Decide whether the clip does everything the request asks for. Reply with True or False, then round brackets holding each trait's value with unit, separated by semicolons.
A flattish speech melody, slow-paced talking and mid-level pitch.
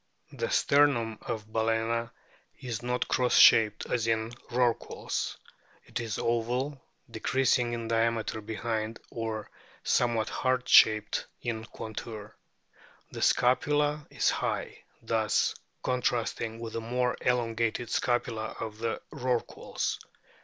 False (1.8 semitones; 110 wpm; 115 Hz)